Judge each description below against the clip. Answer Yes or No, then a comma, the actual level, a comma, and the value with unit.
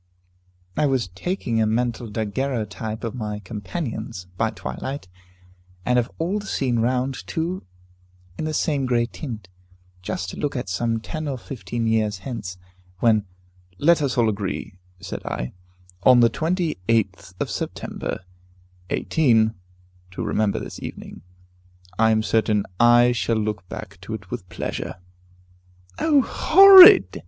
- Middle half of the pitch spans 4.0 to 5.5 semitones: Yes, average, 4.3 semitones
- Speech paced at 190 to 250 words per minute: No, average, 145 wpm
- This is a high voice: No, low, 115 Hz